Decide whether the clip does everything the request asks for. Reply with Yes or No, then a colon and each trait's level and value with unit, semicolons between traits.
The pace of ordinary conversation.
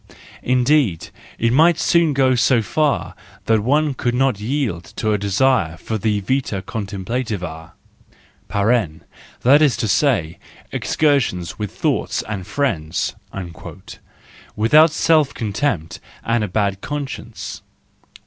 No: slow, 115 wpm